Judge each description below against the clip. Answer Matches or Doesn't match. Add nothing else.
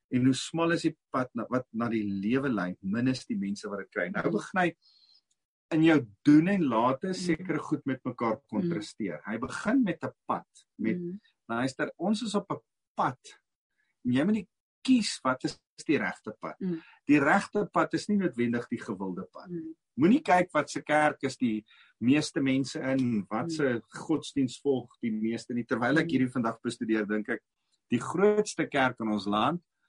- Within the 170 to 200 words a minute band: Matches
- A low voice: Doesn't match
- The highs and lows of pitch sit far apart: Matches